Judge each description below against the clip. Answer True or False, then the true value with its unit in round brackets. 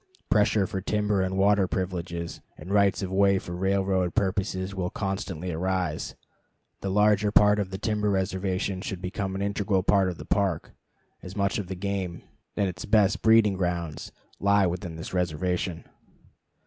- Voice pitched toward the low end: True (95 Hz)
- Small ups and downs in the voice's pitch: True (1.7 semitones)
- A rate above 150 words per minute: True (160 wpm)